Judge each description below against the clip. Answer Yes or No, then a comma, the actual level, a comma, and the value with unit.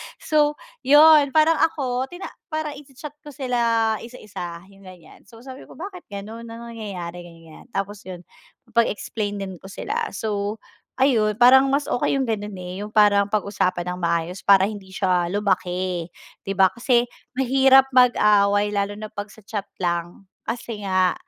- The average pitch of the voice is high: Yes, high, 210 Hz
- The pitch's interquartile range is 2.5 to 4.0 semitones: No, average, 5.3 semitones